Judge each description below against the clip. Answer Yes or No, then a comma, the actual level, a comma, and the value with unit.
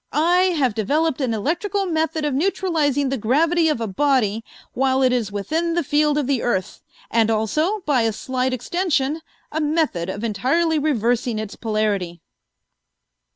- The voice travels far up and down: Yes, wide, 6.0 semitones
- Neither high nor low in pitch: No, very high, 270 Hz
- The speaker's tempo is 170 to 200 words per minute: No, average, 155 wpm